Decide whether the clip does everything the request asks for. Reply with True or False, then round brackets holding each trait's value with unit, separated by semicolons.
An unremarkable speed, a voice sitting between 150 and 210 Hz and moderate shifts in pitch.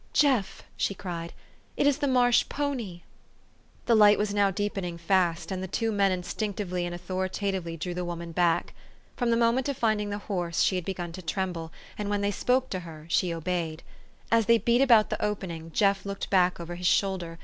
False (210 wpm; 190 Hz; 3.3 semitones)